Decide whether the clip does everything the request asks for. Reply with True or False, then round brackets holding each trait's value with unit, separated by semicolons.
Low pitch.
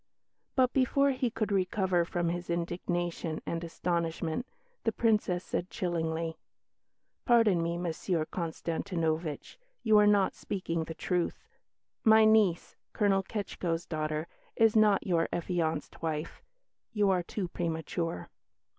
False (175 Hz)